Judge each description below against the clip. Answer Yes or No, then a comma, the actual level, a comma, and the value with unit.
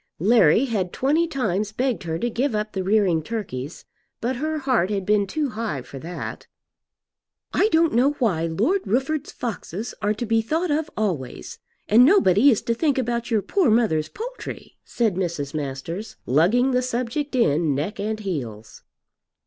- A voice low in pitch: No, high, 220 Hz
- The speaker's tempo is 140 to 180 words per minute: Yes, average, 165 wpm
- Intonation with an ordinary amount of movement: No, wide, 6.7 semitones